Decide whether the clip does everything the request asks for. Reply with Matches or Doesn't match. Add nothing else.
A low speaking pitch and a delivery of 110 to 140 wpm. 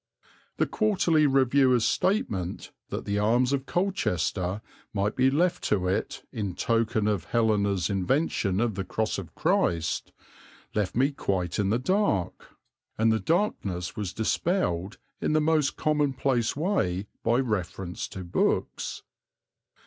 Matches